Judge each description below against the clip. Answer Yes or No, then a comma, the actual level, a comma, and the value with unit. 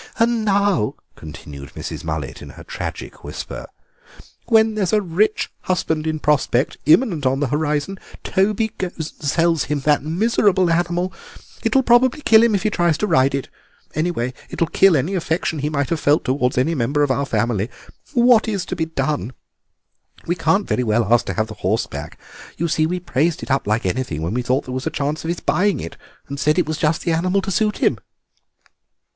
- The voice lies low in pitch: No, medium, 160 Hz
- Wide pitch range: Yes, wide, 6.2 semitones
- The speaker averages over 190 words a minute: Yes, fast, 205 wpm